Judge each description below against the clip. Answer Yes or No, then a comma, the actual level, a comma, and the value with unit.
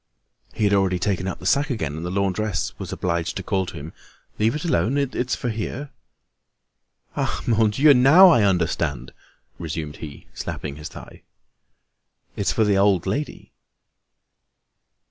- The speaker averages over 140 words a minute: Yes, average, 155 wpm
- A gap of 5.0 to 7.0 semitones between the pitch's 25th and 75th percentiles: Yes, wide, 5.6 semitones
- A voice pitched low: Yes, low, 100 Hz